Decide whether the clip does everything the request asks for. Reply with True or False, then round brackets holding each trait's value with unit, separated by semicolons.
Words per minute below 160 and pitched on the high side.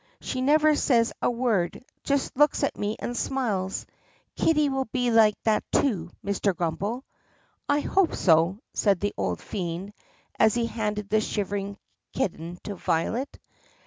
True (150 wpm; 215 Hz)